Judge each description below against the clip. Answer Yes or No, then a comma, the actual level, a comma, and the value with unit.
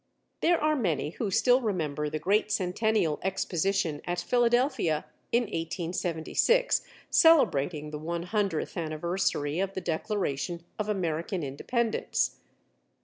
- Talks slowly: Yes, slow, 115 wpm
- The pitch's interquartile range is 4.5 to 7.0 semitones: Yes, wide, 5.6 semitones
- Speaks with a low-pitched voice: No, medium, 180 Hz